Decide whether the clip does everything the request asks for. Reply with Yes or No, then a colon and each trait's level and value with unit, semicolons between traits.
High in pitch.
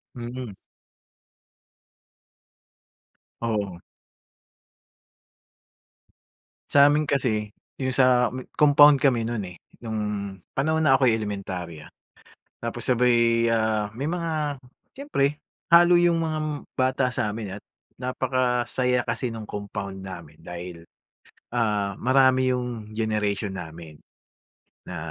No: low, 120 Hz